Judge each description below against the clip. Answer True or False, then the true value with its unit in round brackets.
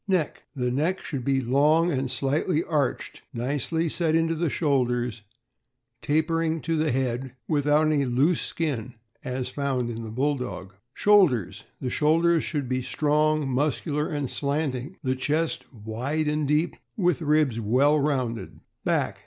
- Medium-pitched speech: True (145 Hz)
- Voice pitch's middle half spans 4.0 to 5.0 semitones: False (3.5 semitones)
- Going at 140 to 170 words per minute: True (150 wpm)